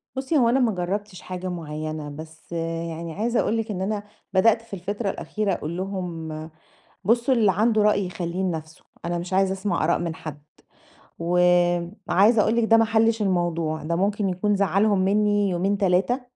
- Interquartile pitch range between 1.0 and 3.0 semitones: No, average, 3.6 semitones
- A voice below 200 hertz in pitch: Yes, high, 190 Hz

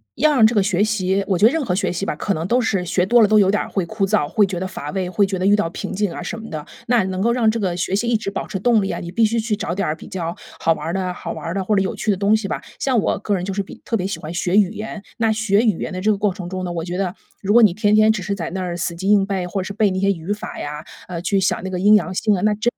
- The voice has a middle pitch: No, high, 195 Hz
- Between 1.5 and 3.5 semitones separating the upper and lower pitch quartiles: Yes, average, 2.8 semitones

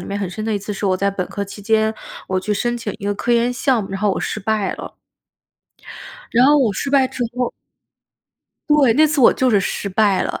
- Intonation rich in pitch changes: No, average, 3.7 semitones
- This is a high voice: Yes, high, 220 Hz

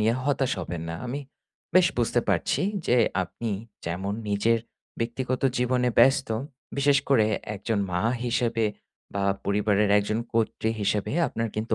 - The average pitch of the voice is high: No, low, 115 Hz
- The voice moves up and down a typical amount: Yes, average, 3.4 semitones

